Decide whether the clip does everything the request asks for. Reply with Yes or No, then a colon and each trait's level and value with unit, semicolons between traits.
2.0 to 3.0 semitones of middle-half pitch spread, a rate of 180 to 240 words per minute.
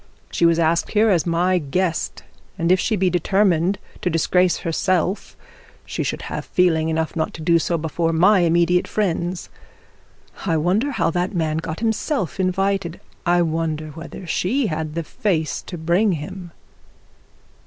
No: narrow, 2.6 semitones; average, 155 wpm